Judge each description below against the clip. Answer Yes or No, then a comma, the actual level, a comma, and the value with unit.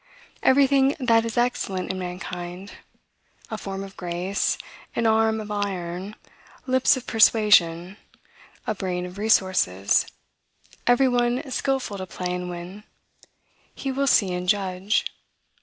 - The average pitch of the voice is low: No, high, 200 Hz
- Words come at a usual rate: No, slow, 125 wpm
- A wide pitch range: No, average, 4.5 semitones